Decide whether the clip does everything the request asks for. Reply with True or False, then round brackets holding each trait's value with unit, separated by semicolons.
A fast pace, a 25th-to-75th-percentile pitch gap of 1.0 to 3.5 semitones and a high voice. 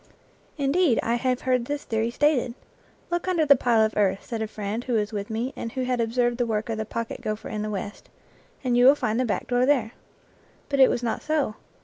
True (245 wpm; 3.0 semitones; 240 Hz)